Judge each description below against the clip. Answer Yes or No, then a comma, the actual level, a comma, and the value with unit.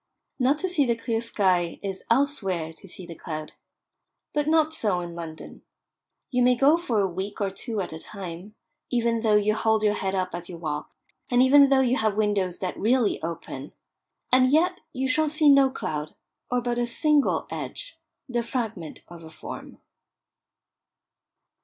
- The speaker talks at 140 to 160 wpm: No, average, 180 wpm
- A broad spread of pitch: Yes, wide, 6.2 semitones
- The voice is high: Yes, high, 220 Hz